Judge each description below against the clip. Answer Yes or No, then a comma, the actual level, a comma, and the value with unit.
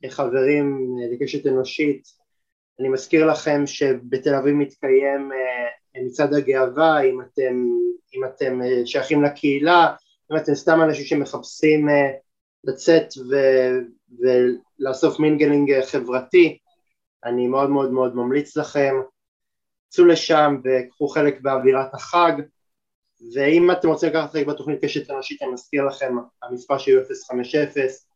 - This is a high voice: No, medium, 140 Hz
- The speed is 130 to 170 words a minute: No, average, 115 wpm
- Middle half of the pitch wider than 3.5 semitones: No, average, 2.8 semitones